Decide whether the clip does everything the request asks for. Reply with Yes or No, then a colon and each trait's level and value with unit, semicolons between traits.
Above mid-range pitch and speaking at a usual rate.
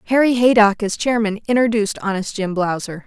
Yes: high, 215 Hz; average, 155 wpm